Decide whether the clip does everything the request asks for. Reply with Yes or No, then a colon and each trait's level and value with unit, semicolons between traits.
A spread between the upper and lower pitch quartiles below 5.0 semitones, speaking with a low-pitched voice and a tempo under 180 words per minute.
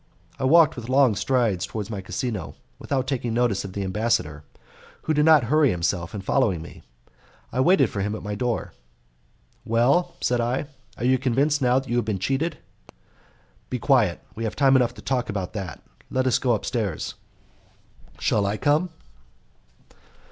Yes: average, 4.5 semitones; low, 120 Hz; average, 170 wpm